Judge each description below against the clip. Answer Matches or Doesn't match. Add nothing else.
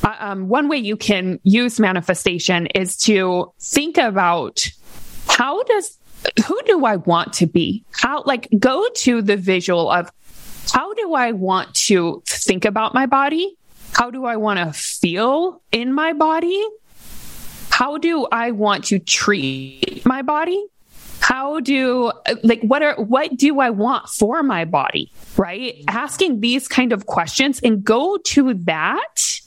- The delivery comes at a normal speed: Matches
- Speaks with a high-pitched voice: Matches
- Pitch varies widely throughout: Matches